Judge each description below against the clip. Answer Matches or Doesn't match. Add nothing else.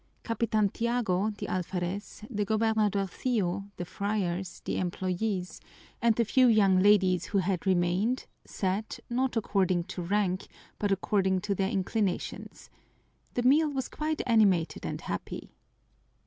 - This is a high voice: Matches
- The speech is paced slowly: Matches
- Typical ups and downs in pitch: Matches